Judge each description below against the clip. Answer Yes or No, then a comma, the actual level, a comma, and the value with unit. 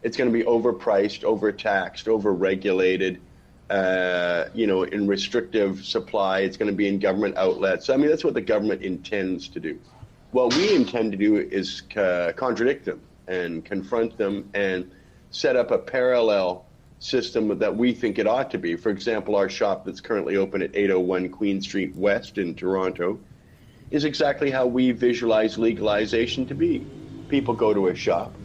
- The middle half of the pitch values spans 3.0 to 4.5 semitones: Yes, average, 4.0 semitones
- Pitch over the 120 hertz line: No, low, 100 Hz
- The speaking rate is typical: Yes, average, 175 wpm